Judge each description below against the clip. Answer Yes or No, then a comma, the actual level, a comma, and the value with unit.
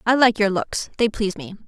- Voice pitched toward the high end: Yes, high, 225 Hz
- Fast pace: Yes, fast, 250 wpm